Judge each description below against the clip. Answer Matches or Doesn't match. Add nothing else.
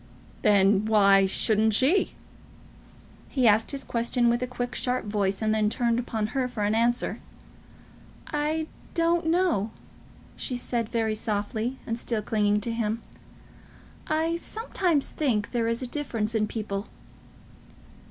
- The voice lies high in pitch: Matches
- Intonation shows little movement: Doesn't match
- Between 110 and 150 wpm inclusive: Matches